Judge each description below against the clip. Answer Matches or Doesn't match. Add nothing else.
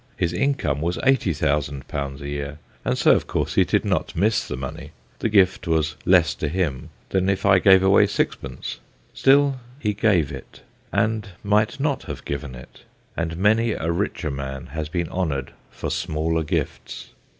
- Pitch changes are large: Matches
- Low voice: Matches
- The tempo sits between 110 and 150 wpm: Doesn't match